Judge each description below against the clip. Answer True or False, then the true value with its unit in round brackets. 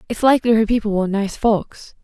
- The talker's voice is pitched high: True (215 Hz)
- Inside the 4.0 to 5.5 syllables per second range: False (6.1 syllables/s)